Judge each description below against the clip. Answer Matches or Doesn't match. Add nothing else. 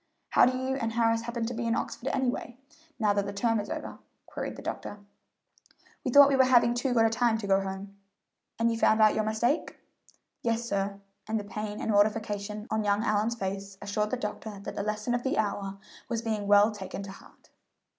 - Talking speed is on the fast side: Matches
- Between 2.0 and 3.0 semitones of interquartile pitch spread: Matches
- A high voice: Matches